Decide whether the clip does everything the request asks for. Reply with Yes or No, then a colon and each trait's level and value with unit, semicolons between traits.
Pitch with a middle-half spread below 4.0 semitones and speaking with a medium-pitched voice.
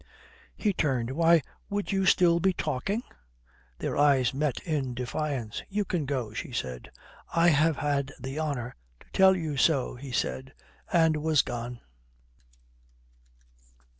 No: average, 4.7 semitones; medium, 145 Hz